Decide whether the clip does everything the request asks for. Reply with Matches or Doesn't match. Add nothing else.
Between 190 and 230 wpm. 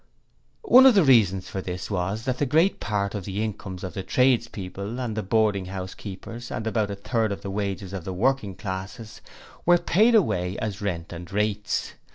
Matches